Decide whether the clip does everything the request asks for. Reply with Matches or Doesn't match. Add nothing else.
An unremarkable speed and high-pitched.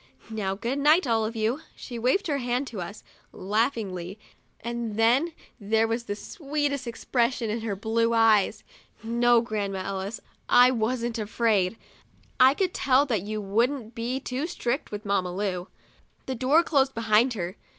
Matches